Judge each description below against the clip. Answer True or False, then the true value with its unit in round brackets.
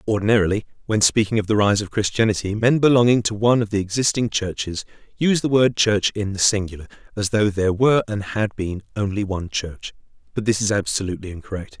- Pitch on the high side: False (105 Hz)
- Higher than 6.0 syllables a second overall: True (6.3 syllables/s)